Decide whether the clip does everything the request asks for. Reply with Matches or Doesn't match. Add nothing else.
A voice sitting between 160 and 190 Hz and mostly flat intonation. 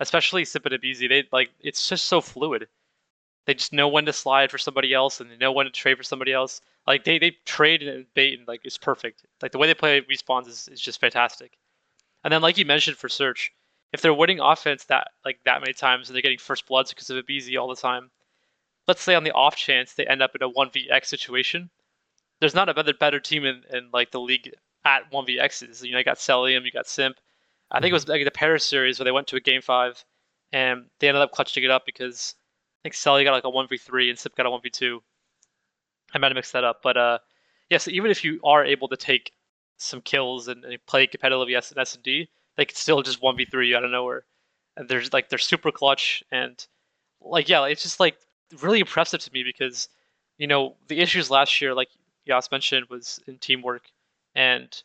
Doesn't match